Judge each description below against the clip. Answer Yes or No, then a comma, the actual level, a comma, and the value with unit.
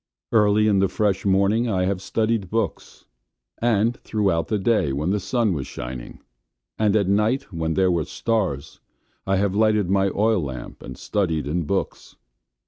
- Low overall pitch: Yes, low, 100 Hz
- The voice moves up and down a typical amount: Yes, average, 3.7 semitones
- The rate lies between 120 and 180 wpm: Yes, average, 170 wpm